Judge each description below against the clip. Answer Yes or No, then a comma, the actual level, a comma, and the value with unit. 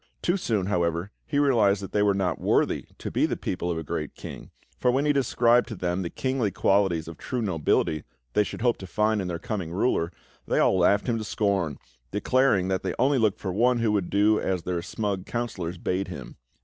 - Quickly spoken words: Yes, fast, 220 wpm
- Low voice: Yes, low, 100 Hz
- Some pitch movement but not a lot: Yes, average, 4.5 semitones